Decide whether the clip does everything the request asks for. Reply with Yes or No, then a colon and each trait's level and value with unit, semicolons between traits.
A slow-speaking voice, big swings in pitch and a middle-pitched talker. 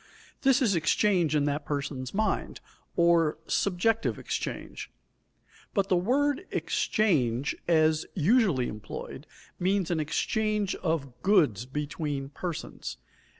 Yes: slow, 105 wpm; wide, 6.0 semitones; medium, 170 Hz